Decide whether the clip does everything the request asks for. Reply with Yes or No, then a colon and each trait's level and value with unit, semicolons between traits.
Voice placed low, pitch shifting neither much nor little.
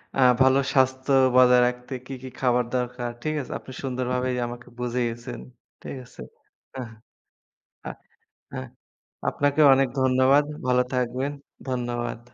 No: low, 125 Hz; narrow, 1.3 semitones